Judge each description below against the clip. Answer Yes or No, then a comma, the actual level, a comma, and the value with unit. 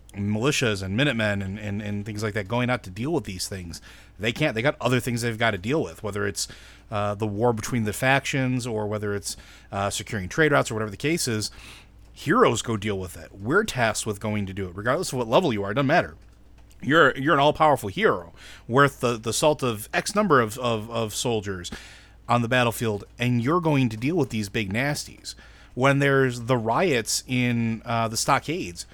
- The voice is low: Yes, low, 115 Hz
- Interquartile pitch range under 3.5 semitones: No, average, 3.8 semitones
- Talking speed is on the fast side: Yes, fast, 220 wpm